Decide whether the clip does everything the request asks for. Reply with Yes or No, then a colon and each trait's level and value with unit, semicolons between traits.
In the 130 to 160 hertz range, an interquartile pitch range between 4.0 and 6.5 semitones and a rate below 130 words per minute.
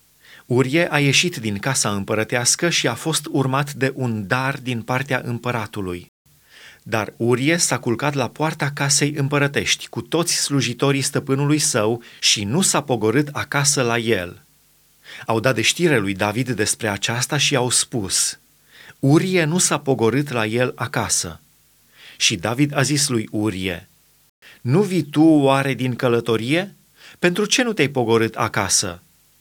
No: low, 135 Hz; average, 4.3 semitones; average, 145 wpm